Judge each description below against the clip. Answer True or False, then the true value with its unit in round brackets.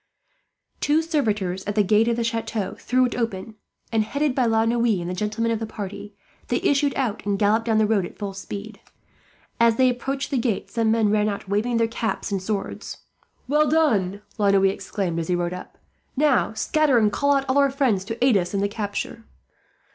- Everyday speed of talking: False (210 wpm)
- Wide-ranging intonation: False (3.5 semitones)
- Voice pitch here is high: True (220 Hz)